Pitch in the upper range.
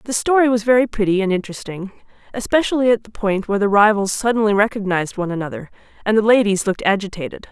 Yes: high, 210 Hz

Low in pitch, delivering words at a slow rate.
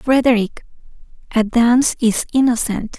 No: high, 235 Hz; slow, 100 wpm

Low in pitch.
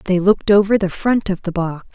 No: high, 190 Hz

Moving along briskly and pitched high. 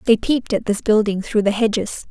Yes: fast, 230 wpm; high, 215 Hz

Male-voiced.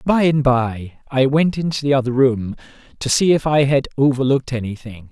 Yes: male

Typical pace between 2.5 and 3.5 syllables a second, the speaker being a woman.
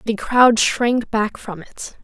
Yes: 3.2 syllables/s; female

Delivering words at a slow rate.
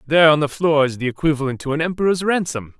No: fast, 235 wpm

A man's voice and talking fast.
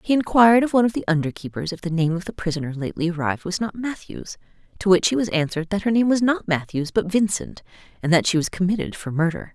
No: female; fast, 240 wpm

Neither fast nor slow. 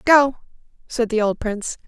Yes: average, 160 wpm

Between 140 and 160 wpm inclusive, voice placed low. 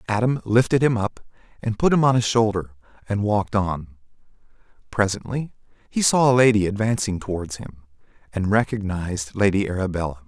Yes: average, 145 wpm; low, 105 Hz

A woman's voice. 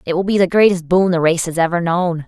Yes: female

